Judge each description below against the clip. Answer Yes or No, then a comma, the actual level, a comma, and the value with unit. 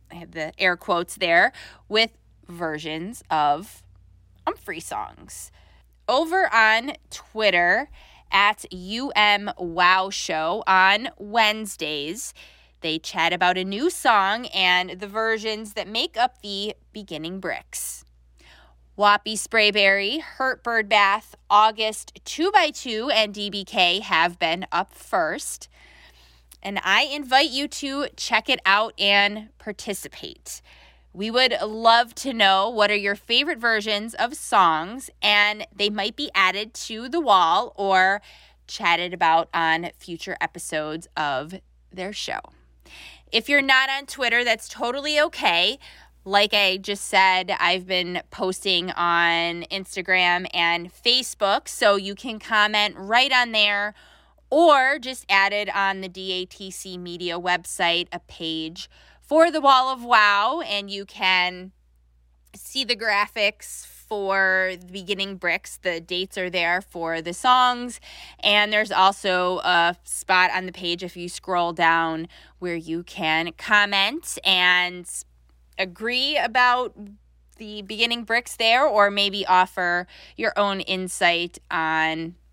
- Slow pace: Yes, slow, 125 wpm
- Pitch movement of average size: Yes, average, 4.2 semitones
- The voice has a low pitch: No, high, 195 Hz